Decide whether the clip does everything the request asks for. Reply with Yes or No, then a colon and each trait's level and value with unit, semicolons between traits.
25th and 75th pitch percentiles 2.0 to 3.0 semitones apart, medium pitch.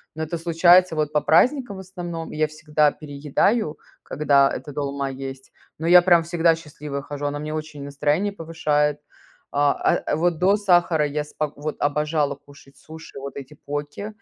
Yes: narrow, 2.6 semitones; medium, 150 Hz